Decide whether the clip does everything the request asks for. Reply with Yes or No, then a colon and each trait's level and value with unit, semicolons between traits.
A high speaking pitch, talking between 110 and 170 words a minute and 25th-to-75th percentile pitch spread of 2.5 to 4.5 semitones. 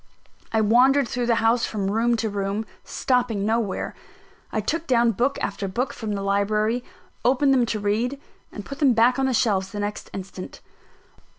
No: high, 225 Hz; average, 180 wpm; average, 3.4 semitones